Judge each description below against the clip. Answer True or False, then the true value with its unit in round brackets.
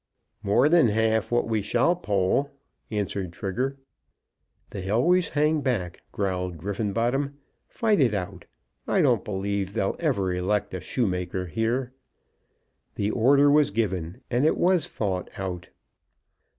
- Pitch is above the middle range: False (110 Hz)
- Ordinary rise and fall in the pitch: False (5.9 semitones)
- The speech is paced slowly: True (130 wpm)